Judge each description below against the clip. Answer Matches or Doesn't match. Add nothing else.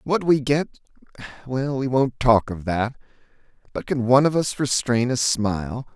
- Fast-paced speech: Doesn't match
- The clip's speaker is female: Doesn't match